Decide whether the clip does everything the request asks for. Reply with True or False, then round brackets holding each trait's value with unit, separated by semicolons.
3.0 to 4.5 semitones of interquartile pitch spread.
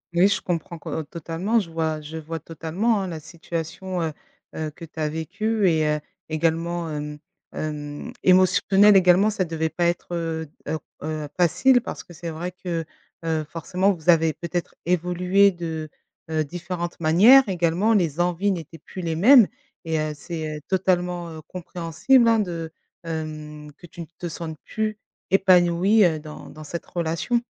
False (2.6 semitones)